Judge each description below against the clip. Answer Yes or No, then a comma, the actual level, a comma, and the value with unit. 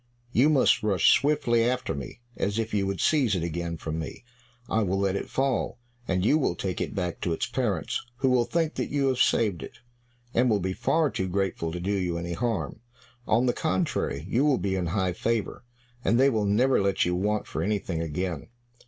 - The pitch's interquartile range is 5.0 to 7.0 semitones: Yes, wide, 5.5 semitones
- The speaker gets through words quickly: Yes, fast, 215 wpm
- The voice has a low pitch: Yes, low, 100 Hz